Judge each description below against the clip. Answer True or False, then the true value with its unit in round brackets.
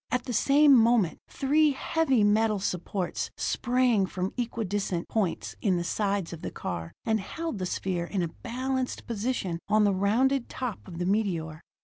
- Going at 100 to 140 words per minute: False (170 wpm)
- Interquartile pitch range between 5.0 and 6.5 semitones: True (5.4 semitones)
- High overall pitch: True (210 Hz)